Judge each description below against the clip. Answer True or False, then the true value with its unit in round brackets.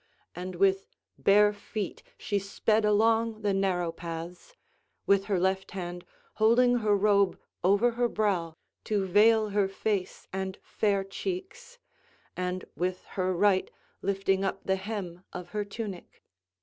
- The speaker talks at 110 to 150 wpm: True (135 wpm)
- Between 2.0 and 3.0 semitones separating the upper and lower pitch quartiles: True (2.5 semitones)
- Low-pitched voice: False (195 Hz)